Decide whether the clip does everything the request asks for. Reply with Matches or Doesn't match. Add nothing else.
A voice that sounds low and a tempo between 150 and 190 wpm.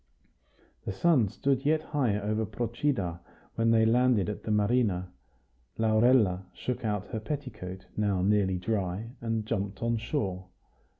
Doesn't match